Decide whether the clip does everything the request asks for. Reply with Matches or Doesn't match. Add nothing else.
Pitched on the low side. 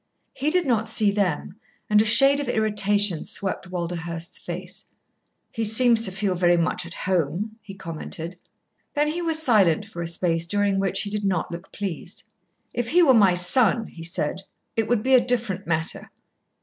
Doesn't match